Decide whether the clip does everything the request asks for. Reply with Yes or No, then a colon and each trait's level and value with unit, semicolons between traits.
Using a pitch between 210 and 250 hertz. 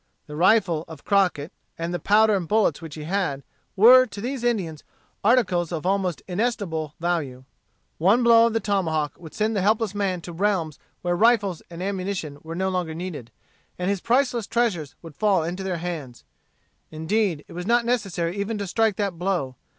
No: medium, 185 Hz